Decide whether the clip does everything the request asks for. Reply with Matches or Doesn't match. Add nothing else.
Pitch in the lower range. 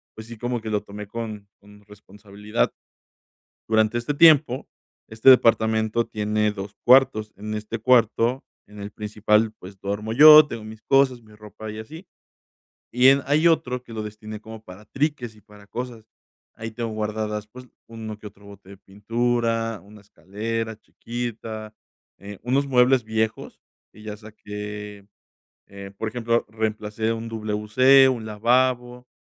Matches